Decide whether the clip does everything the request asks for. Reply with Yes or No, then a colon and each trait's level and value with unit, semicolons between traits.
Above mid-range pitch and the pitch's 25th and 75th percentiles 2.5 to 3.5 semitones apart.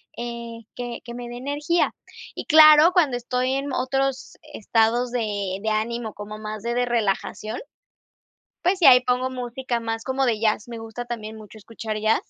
Yes: high, 240 Hz; average, 2.8 semitones